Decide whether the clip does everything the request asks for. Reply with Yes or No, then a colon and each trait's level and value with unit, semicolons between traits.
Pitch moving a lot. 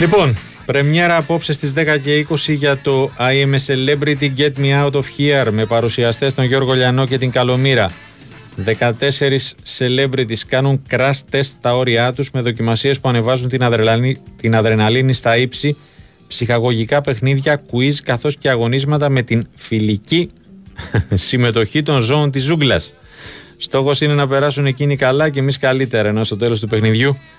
No: average, 3.1 semitones